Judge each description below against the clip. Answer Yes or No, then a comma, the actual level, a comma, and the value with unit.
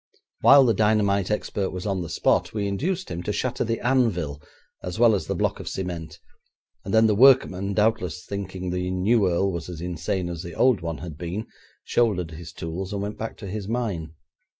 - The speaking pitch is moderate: No, very low, 95 Hz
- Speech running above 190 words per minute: Yes, average, 200 wpm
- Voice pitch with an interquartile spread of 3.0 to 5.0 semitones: Yes, average, 3.9 semitones